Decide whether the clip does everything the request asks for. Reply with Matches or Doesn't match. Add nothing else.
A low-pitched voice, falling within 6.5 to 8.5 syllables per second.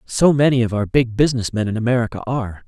Matches